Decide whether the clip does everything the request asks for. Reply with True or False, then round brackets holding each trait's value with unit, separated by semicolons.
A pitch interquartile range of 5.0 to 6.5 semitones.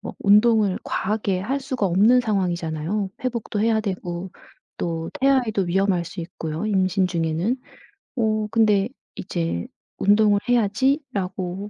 False (3.6 semitones)